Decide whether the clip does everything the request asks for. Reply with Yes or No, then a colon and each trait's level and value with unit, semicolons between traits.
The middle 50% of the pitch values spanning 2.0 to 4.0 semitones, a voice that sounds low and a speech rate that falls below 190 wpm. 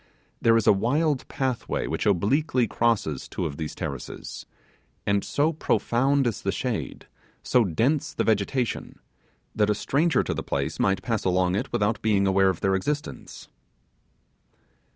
No: average, 5.3 semitones; low, 110 Hz; average, 155 wpm